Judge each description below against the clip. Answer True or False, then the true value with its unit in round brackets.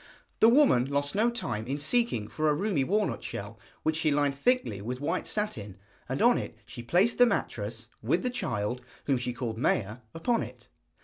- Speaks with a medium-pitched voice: True (145 Hz)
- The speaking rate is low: False (190 wpm)